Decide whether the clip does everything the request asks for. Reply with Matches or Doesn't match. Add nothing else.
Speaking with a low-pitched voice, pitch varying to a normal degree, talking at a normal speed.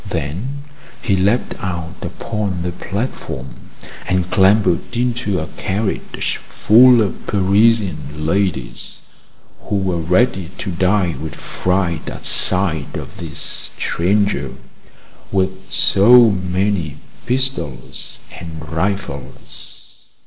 Doesn't match